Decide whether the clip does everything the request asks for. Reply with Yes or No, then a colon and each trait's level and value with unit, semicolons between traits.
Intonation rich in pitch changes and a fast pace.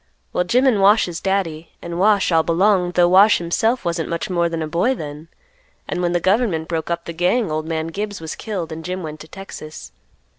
No: average, 3.3 semitones; fast, 215 wpm